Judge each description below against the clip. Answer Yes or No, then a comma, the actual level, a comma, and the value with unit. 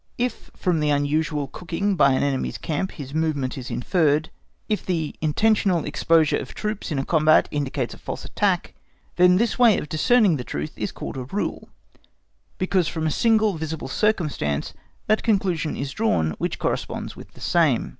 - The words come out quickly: No, average, 170 wpm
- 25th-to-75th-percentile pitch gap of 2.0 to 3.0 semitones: No, average, 5.2 semitones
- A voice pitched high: No, medium, 160 Hz